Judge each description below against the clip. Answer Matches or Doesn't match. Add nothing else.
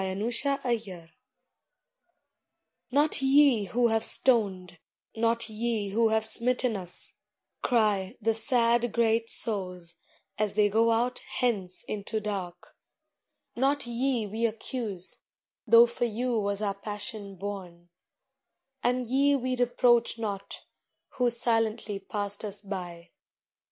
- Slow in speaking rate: Matches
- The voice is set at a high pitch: Matches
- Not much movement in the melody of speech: Doesn't match